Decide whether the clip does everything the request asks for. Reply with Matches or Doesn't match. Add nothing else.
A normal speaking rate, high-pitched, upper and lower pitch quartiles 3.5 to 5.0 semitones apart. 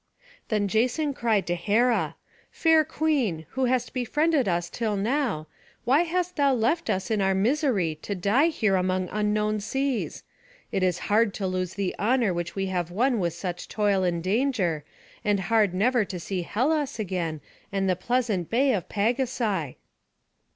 Doesn't match